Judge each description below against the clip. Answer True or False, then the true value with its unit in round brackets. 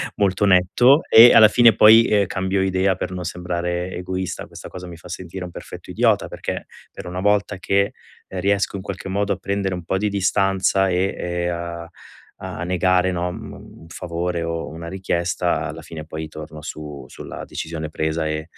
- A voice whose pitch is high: False (90 Hz)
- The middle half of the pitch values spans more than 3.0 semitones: False (2.5 semitones)